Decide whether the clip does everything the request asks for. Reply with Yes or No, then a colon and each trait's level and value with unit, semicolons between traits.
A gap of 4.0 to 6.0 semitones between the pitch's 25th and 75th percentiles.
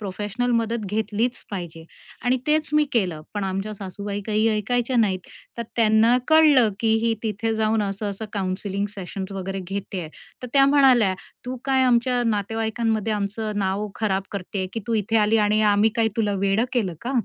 No: average, 2.8 semitones